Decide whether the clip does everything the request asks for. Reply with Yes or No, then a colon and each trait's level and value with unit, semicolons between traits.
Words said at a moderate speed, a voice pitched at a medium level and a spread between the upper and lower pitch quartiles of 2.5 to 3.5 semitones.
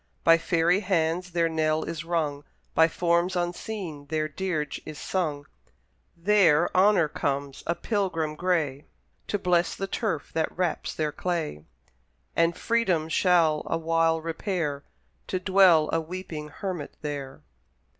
No: slow, 130 wpm; medium, 165 Hz; average, 2.9 semitones